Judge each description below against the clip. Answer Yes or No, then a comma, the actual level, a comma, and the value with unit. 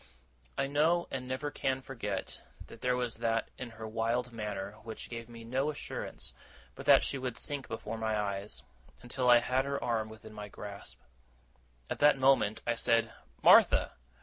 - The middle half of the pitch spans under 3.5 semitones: Yes, average, 3.1 semitones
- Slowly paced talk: No, average, 175 wpm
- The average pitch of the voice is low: Yes, low, 120 Hz